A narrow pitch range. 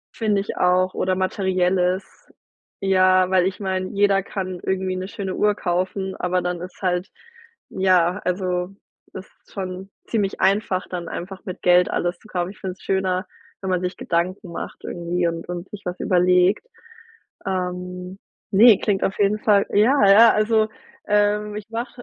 Yes: narrow, 1.7 semitones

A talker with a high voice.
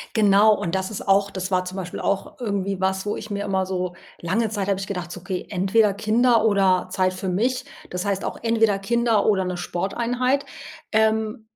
Yes: high, 200 Hz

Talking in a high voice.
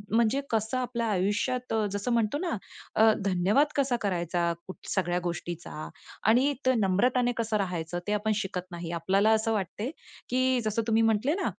Yes: high, 215 Hz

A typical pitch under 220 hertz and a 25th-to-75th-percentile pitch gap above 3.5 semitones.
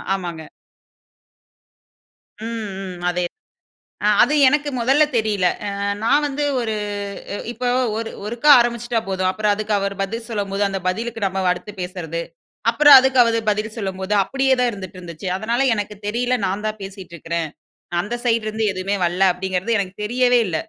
Yes: high, 210 Hz; average, 3.9 semitones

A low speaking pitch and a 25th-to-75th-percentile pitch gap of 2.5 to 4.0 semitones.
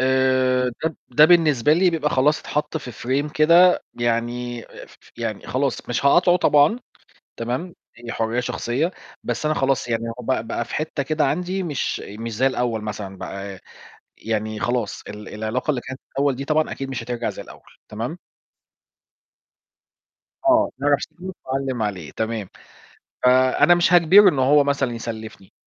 No: low, 130 Hz; average, 4.7 semitones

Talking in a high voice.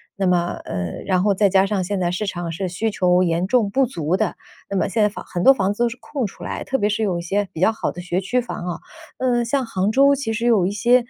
Yes: high, 200 Hz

